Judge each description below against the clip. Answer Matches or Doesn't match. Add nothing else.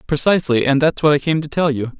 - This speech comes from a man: Matches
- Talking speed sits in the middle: Doesn't match